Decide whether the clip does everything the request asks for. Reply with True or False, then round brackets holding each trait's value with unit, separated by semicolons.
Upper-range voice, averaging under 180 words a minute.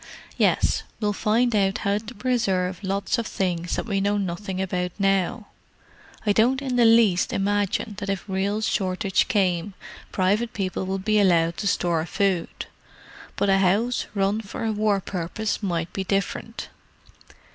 True (200 Hz; 155 wpm)